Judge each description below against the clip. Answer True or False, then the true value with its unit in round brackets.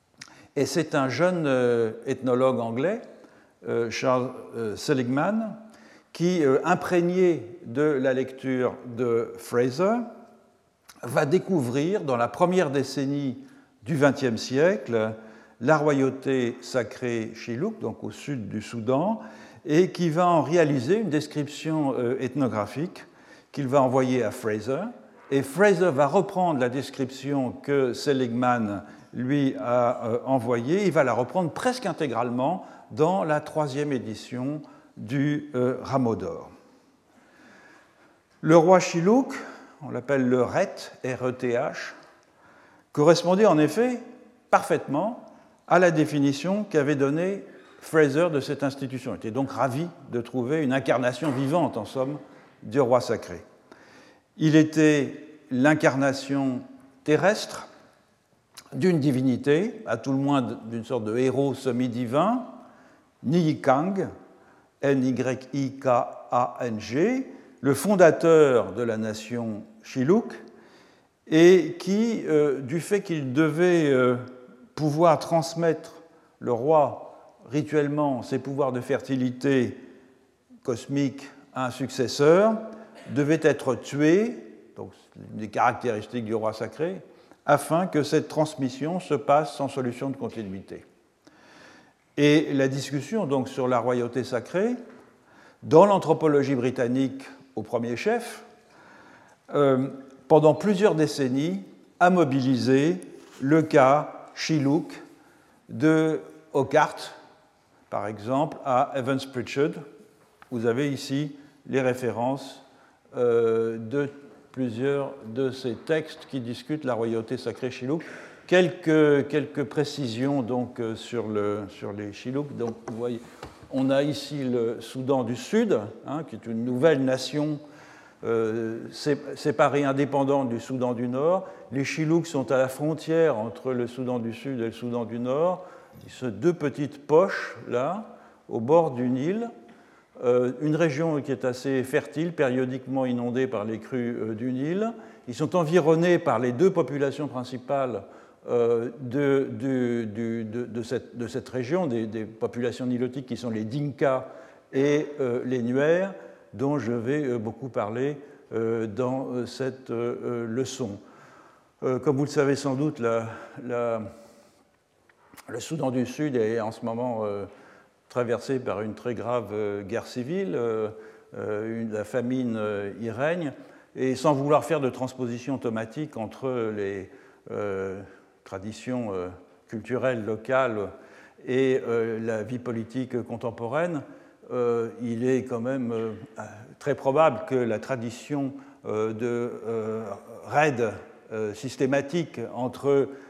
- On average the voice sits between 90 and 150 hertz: True (135 Hz)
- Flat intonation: False (3.9 semitones)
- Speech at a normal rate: False (125 wpm)